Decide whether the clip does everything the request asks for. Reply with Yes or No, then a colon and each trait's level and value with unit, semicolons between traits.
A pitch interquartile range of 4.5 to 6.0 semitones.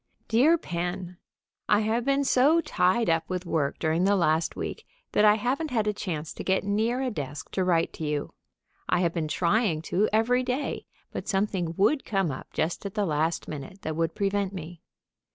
Yes: average, 5.0 semitones